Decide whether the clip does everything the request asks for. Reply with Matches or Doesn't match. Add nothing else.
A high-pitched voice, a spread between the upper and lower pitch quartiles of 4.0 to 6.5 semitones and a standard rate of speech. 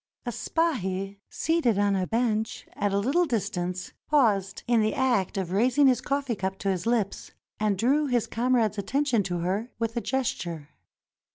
Matches